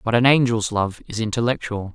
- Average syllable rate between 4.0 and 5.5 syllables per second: No, 5.7 syllables/s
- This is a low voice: Yes, low, 115 Hz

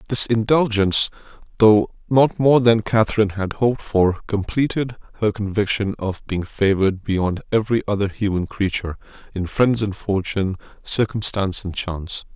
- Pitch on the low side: Yes, low, 105 Hz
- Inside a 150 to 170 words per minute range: No, slow, 135 wpm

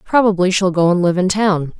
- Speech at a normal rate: No, fast, 235 wpm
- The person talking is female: Yes, female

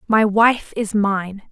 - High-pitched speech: Yes, high, 210 Hz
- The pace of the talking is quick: No, average, 160 wpm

